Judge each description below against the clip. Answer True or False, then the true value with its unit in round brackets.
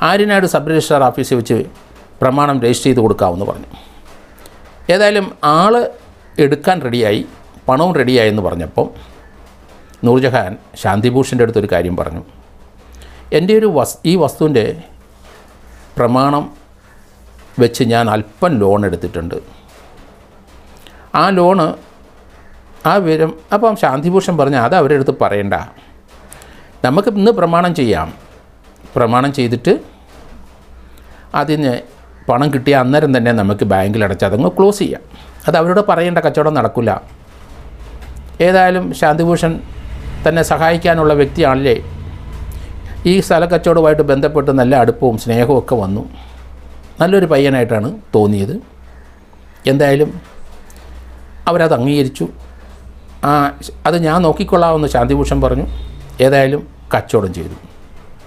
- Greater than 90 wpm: True (100 wpm)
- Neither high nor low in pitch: False (120 Hz)